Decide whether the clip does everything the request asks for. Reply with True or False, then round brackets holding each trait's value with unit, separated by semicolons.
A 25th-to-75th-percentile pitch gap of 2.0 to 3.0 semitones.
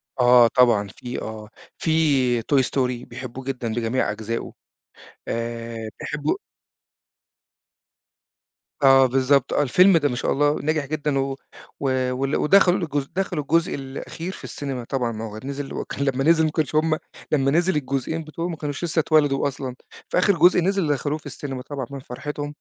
False (3.6 semitones)